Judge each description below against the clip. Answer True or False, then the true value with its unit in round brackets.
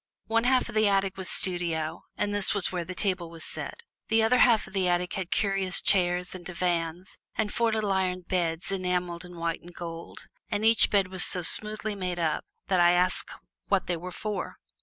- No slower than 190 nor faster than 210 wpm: True (205 wpm)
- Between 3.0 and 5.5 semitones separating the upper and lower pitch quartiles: False (2.6 semitones)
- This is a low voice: False (185 Hz)